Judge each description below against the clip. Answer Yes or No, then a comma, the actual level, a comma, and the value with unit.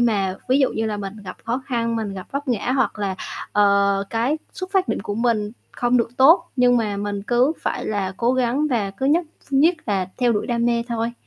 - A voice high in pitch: Yes, high, 235 Hz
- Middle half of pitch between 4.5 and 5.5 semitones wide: No, average, 3.9 semitones